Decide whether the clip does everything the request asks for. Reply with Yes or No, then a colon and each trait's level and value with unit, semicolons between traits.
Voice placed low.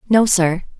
No: high, 190 Hz